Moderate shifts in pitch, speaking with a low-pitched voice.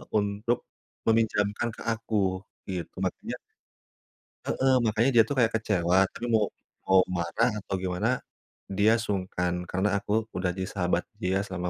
Yes: average, 3.4 semitones; low, 100 Hz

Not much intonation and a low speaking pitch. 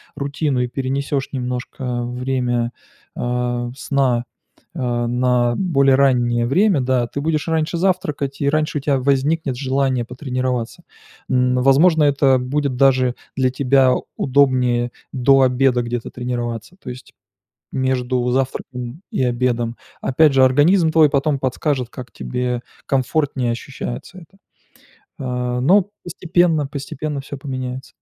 Yes: narrow, 2.3 semitones; low, 130 Hz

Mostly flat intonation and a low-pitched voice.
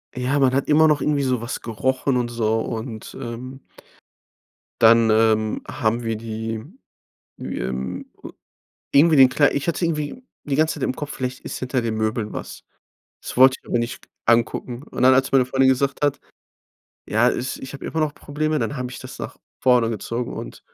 No: average, 3.3 semitones; low, 125 Hz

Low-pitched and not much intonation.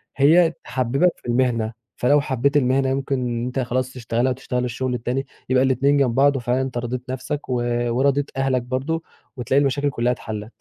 Yes: low, 130 Hz; narrow, 2.0 semitones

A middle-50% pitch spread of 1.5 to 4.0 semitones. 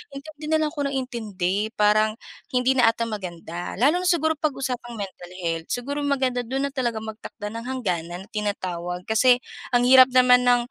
No: average, 4.5 semitones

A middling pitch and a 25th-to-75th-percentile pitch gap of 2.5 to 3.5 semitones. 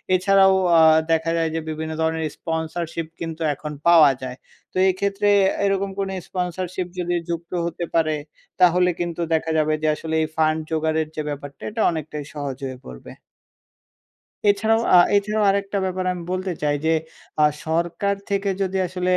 Yes: medium, 170 Hz; average, 3.0 semitones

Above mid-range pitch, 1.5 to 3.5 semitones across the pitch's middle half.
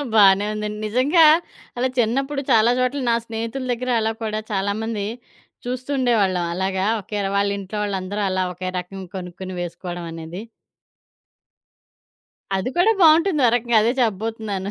No: high, 210 Hz; average, 4.1 semitones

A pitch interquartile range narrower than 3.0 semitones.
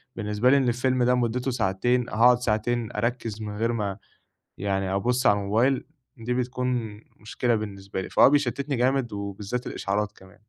No: average, 3.3 semitones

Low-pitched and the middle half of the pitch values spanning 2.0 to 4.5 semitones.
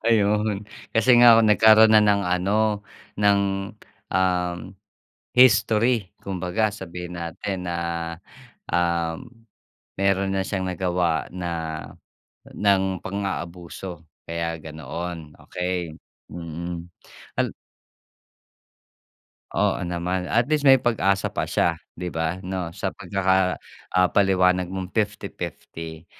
Yes: very low, 95 Hz; average, 2.9 semitones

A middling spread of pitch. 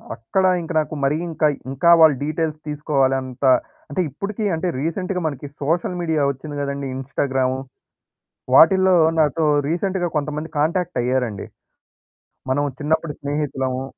Yes: average, 3.3 semitones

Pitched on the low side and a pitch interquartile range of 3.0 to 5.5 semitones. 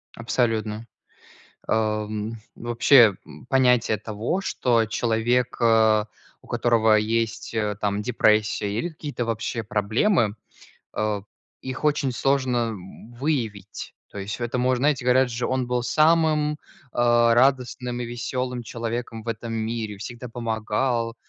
No: low, 115 Hz; narrow, 2.5 semitones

